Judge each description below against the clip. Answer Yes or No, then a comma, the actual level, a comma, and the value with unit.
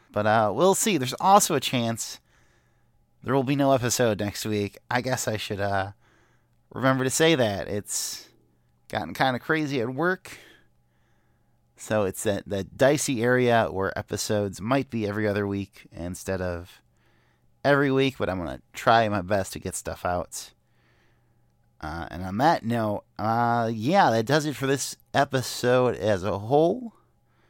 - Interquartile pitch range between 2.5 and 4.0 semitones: No, average, 4.4 semitones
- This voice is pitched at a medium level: No, low, 115 Hz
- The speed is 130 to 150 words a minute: No, average, 165 wpm